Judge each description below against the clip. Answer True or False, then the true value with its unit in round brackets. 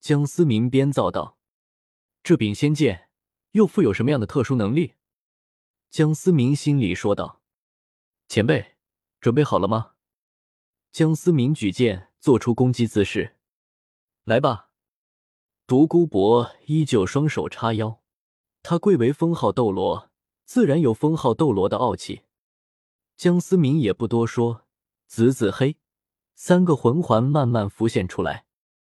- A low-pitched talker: True (120 Hz)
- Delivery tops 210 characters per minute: False (195 characters per minute)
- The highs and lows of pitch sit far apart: True (7.1 semitones)